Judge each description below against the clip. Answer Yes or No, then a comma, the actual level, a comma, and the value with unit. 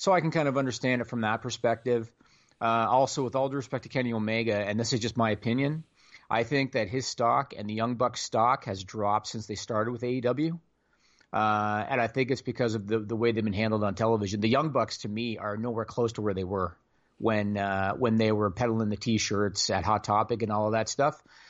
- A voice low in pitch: Yes, low, 115 Hz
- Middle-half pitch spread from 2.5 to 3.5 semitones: Yes, average, 2.8 semitones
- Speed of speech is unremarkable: No, fast, 235 wpm